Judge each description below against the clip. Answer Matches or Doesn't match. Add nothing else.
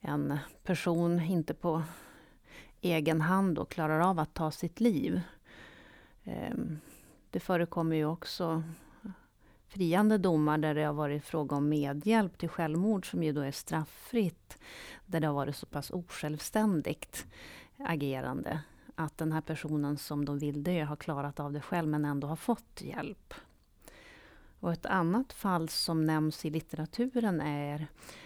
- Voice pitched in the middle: Matches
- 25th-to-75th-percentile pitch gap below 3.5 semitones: Matches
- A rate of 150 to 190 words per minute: Doesn't match